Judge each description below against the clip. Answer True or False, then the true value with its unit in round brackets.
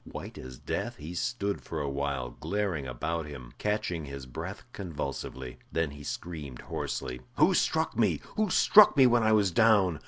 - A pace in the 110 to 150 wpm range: False (175 wpm)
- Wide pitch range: True (6.9 semitones)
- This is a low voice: True (80 Hz)